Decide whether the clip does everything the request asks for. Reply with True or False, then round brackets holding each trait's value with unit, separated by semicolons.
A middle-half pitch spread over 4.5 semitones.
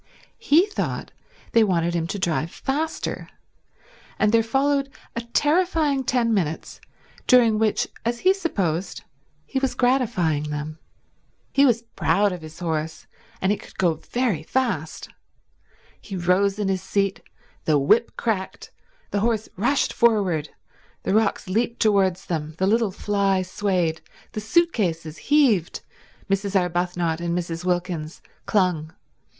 True (5.5 semitones)